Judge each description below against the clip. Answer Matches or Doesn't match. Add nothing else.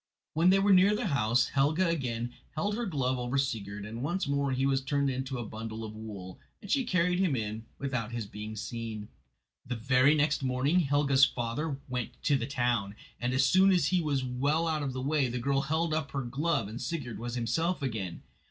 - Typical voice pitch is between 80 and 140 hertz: Matches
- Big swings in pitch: Doesn't match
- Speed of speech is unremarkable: Doesn't match